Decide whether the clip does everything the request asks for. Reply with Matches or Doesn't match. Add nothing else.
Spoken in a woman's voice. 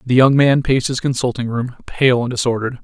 Doesn't match